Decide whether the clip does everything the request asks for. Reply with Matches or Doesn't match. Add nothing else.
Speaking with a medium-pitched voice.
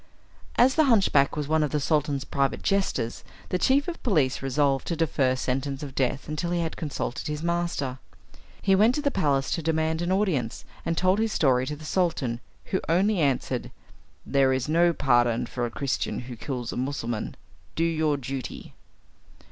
Matches